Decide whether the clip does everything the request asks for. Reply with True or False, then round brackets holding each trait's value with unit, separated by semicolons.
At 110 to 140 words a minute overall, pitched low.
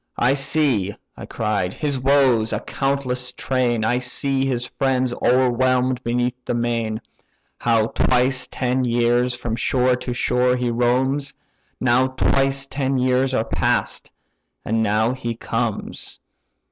True (135 wpm; 125 Hz)